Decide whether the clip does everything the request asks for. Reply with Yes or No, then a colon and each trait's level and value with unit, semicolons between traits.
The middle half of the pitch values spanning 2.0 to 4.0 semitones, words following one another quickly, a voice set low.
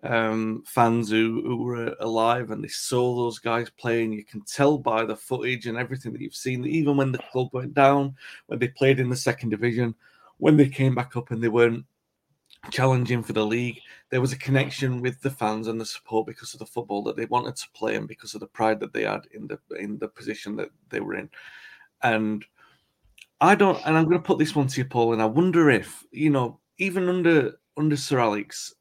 Yes: average, 3.1 semitones; fast, 225 wpm; low, 125 Hz